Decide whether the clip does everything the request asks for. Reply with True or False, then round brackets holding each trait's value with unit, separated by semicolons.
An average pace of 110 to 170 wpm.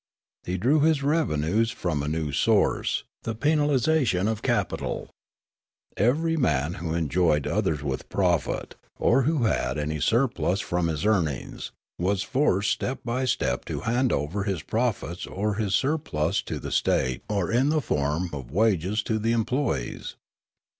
True (155 wpm)